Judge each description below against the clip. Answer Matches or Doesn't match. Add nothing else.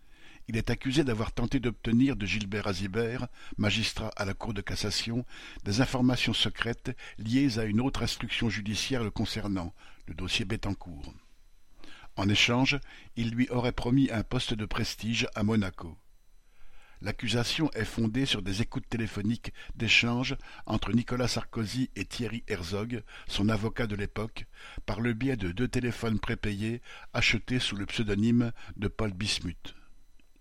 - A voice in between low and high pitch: Doesn't match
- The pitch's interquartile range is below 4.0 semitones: Matches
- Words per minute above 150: Doesn't match